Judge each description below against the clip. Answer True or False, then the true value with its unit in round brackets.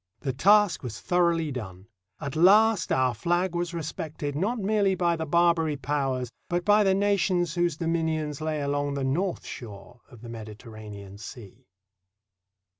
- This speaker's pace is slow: False (150 wpm)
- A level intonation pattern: False (5.3 semitones)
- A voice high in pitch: False (155 Hz)